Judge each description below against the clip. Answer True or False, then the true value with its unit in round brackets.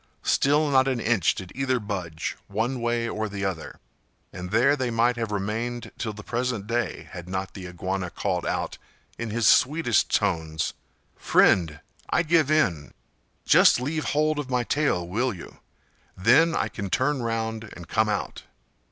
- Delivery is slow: False (165 wpm)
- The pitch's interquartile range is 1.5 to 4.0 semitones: False (5.1 semitones)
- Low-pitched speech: True (115 Hz)